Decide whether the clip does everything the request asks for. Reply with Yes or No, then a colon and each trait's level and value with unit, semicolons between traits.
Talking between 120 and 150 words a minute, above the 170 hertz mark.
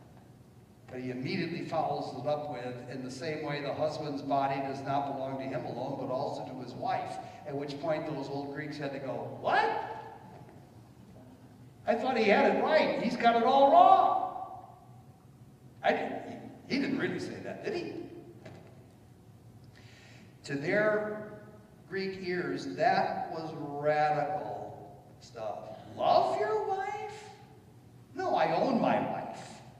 No: average, 145 wpm; medium, 150 Hz